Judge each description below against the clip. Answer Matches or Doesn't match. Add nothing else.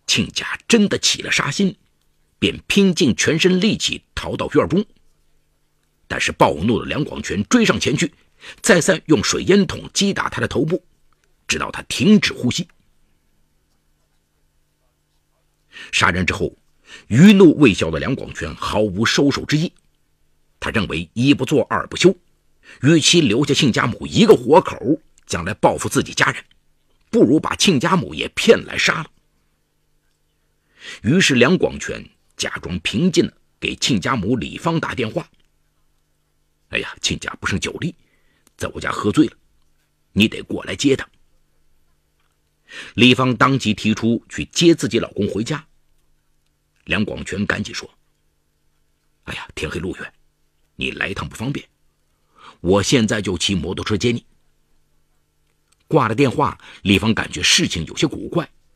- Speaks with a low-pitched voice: Matches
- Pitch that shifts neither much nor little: Doesn't match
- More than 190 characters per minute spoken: Matches